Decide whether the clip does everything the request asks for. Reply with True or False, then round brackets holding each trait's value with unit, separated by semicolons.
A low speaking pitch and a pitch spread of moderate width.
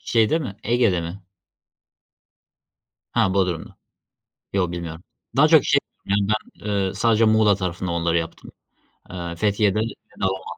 True (95 Hz; 3.7 semitones)